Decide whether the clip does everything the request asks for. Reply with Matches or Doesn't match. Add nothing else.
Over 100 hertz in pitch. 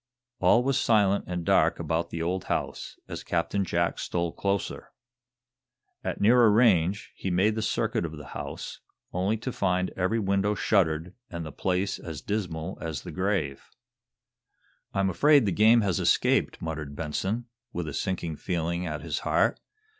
Doesn't match